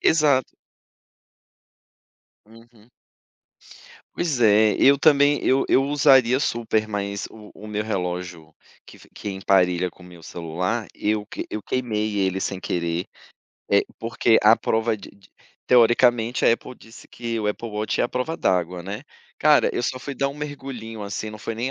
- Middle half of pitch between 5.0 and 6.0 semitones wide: No, average, 4.2 semitones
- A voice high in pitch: No, low, 110 Hz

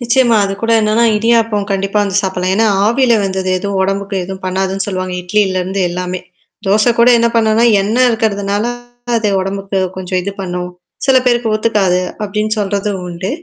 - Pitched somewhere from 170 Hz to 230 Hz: Yes, high, 200 Hz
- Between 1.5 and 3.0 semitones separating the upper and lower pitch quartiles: Yes, average, 2.7 semitones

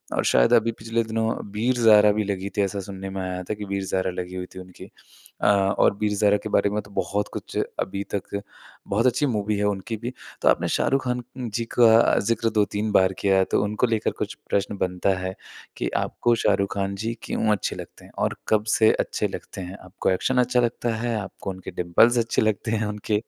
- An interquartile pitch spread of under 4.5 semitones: Yes, average, 2.7 semitones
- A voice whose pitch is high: No, low, 105 Hz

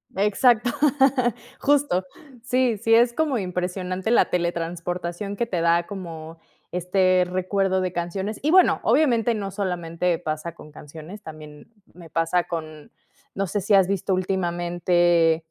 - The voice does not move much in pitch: No, average, 3.1 semitones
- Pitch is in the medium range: Yes, medium, 180 Hz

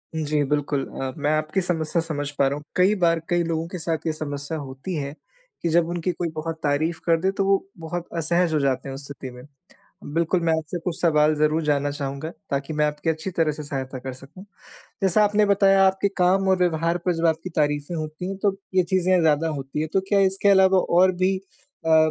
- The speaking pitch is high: No, medium, 160 Hz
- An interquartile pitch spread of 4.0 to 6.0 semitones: No, average, 3.4 semitones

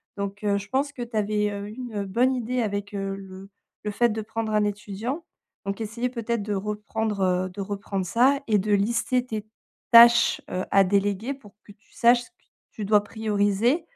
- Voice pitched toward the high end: Yes, high, 210 Hz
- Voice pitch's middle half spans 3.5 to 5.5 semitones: No, average, 2.8 semitones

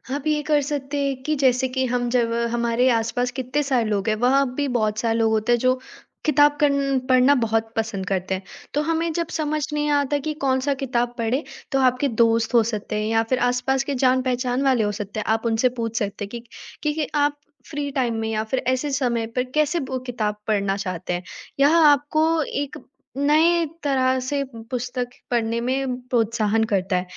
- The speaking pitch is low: No, very high, 250 Hz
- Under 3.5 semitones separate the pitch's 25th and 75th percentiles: No, average, 3.8 semitones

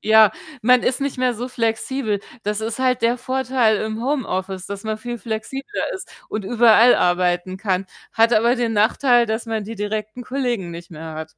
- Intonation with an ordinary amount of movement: Yes, average, 3.2 semitones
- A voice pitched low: No, high, 225 Hz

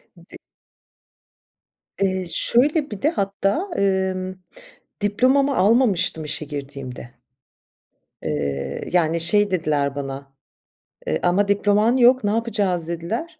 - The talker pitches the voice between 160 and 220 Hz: Yes, high, 190 Hz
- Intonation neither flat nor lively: No, wide, 6.4 semitones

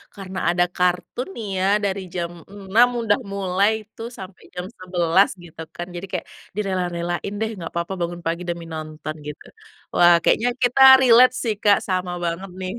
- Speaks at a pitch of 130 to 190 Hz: Yes, medium, 185 Hz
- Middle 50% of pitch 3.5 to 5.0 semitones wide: No, average, 2.7 semitones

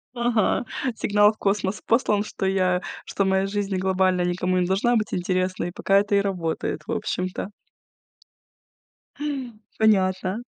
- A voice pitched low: No, high, 190 Hz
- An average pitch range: No, narrow, 2.0 semitones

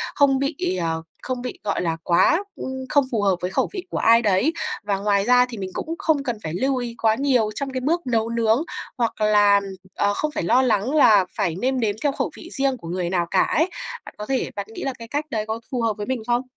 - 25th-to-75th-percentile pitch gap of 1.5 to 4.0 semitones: No, average, 4.8 semitones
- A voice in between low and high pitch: No, high, 230 Hz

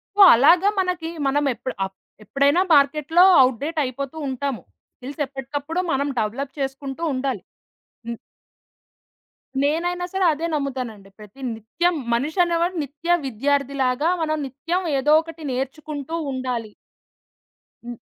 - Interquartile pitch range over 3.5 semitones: Yes, average, 4.0 semitones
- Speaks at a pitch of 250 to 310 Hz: Yes, very high, 280 Hz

